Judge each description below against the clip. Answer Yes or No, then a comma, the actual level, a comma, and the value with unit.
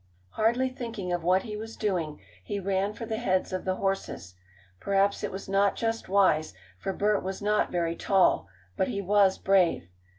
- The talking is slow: No, average, 185 wpm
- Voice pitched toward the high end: Yes, high, 195 Hz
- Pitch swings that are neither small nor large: No, narrow, 2.2 semitones